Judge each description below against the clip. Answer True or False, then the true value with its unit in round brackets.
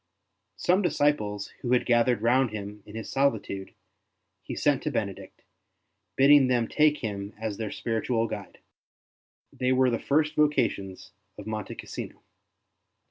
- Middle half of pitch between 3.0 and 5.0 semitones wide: True (4.5 semitones)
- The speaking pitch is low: True (120 Hz)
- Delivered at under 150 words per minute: True (135 wpm)